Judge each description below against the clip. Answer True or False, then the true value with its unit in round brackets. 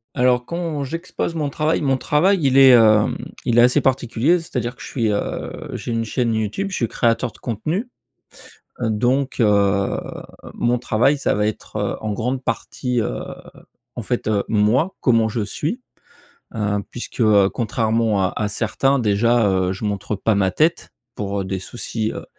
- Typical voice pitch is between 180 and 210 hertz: False (115 Hz)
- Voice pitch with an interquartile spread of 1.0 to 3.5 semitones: False (4.2 semitones)